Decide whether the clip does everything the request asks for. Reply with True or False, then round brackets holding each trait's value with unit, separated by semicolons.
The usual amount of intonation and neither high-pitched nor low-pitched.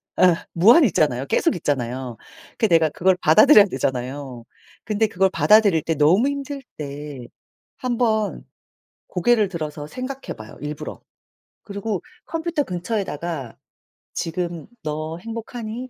False (7.0 semitones; 175 Hz)